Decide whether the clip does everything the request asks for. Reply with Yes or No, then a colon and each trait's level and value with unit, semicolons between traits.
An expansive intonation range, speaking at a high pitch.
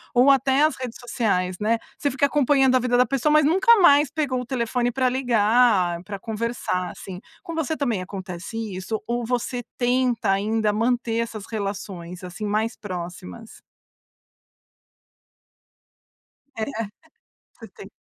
No: average, 4.0 semitones; high, 235 Hz